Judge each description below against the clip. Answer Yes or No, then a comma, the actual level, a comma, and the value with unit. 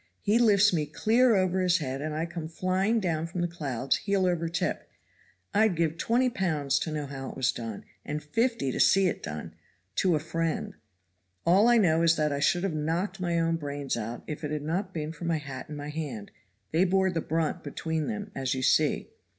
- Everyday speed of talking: No, fast, 215 wpm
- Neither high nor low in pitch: Yes, medium, 165 Hz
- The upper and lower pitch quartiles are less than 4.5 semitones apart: Yes, average, 4.0 semitones